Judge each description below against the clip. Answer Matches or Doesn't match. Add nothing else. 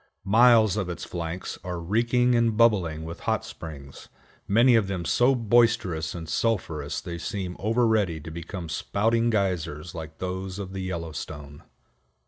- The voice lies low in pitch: Matches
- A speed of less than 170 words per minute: Matches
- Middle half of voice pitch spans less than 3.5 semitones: Doesn't match